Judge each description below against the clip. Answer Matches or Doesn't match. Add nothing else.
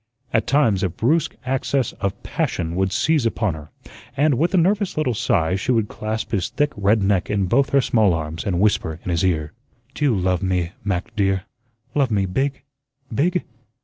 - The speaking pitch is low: Matches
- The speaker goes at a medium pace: Matches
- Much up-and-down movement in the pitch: Matches